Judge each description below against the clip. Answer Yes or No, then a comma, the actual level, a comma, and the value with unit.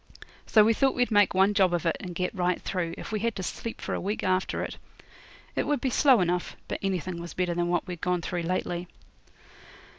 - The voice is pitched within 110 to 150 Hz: No, medium, 185 Hz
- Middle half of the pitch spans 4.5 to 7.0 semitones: No, average, 3.0 semitones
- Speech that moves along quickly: Yes, fast, 230 wpm